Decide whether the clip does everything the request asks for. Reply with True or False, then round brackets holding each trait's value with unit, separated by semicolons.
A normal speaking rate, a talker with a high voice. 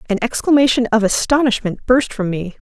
True (155 wpm; 230 Hz)